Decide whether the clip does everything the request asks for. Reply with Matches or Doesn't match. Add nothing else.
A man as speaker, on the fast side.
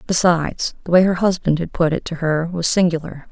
Doesn't match